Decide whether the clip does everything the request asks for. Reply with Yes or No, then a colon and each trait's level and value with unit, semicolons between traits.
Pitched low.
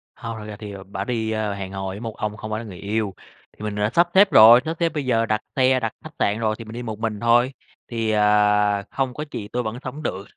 Yes: low, 110 Hz